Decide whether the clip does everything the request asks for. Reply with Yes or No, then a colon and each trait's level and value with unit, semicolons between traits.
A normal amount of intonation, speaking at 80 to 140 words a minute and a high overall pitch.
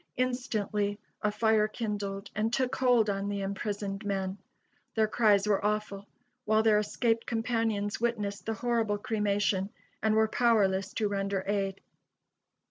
No: narrow, 2.0 semitones; slow, 135 wpm; high, 210 Hz